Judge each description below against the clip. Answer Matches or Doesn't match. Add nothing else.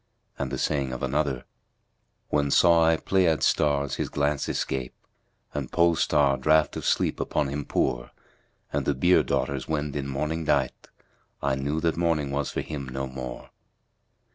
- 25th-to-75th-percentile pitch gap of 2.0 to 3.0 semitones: Matches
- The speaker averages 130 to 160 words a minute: Doesn't match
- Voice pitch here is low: Matches